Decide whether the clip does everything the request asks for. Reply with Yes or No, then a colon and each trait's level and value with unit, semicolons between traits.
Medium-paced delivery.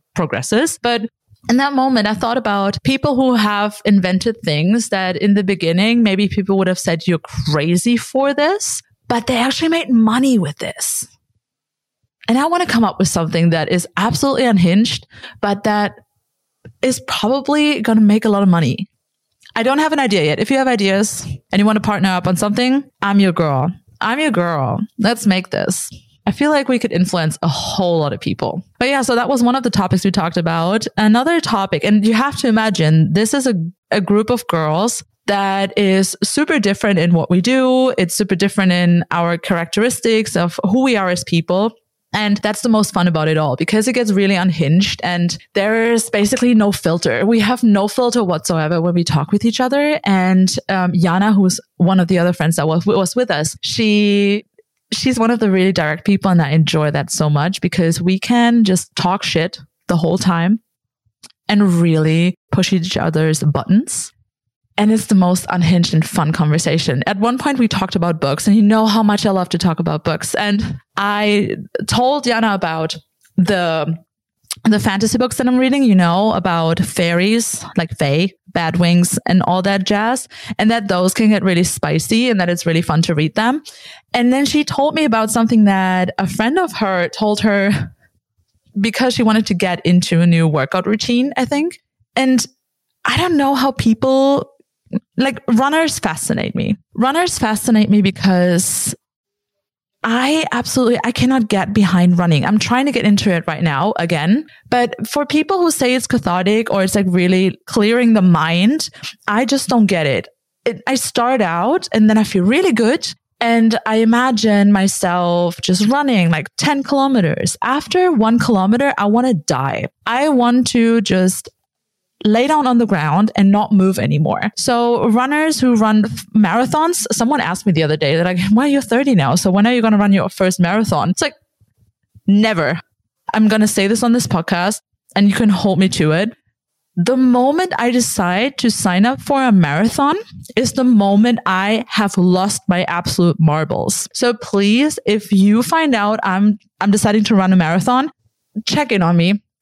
Yes: average, 190 wpm